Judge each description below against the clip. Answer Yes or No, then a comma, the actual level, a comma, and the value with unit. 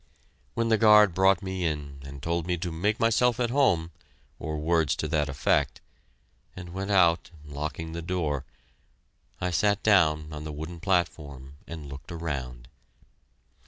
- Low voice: Yes, very low, 85 Hz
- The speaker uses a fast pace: No, average, 155 wpm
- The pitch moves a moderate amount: Yes, average, 4.1 semitones